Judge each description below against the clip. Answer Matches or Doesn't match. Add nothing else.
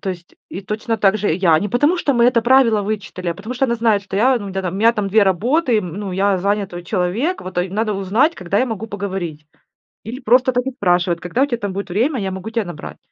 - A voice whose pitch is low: Doesn't match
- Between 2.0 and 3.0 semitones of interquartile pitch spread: Doesn't match